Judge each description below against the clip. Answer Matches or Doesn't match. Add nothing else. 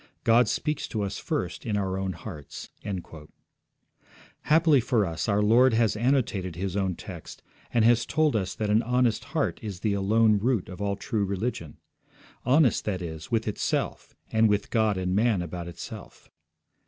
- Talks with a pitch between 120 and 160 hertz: Doesn't match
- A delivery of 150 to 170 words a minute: Matches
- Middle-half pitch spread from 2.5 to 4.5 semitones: Matches